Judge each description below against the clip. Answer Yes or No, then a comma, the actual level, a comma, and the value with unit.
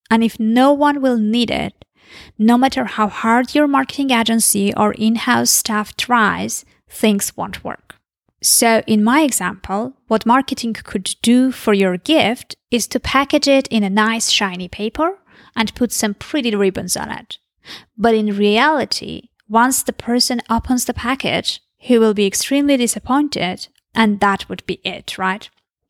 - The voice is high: Yes, high, 230 Hz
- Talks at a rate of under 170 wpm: Yes, average, 160 wpm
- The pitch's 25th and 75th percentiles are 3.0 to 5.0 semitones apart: Yes, average, 3.5 semitones